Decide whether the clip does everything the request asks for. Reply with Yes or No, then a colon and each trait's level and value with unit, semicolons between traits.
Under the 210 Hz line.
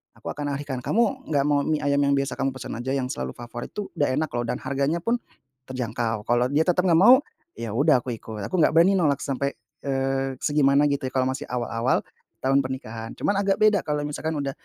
Yes: medium, 140 Hz